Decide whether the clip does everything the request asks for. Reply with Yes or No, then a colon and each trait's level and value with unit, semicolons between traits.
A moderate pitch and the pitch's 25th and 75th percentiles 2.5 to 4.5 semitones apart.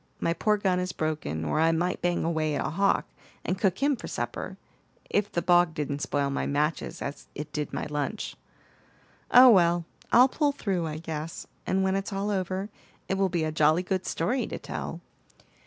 Yes: medium, 175 Hz; average, 3.9 semitones